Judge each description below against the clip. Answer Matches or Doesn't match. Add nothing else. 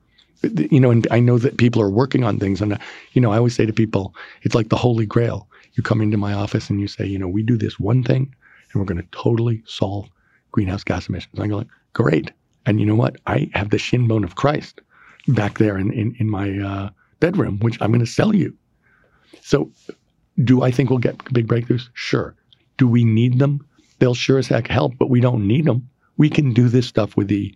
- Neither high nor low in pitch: Doesn't match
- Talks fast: Matches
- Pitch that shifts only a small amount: Doesn't match